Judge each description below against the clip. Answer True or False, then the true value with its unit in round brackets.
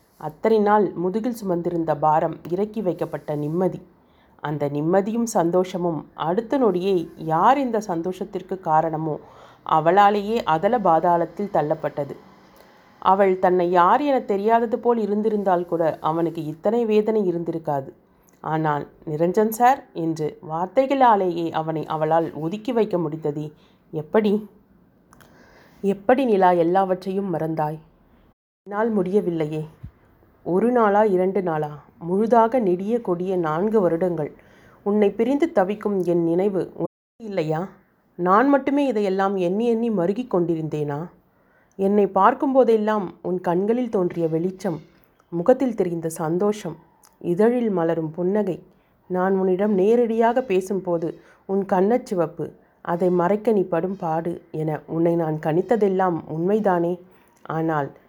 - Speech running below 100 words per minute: False (105 wpm)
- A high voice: False (180 Hz)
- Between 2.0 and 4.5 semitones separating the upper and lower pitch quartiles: True (4.1 semitones)